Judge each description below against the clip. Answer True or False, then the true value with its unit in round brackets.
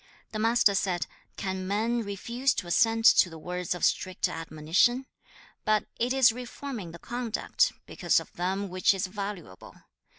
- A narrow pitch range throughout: False (4.6 semitones)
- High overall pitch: True (200 Hz)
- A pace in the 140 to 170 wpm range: True (155 wpm)